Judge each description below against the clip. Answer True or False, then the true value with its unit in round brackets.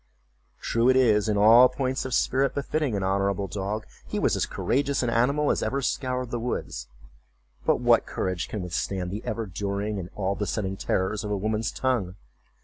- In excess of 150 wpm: True (180 wpm)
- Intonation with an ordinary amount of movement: True (4.8 semitones)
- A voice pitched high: False (105 Hz)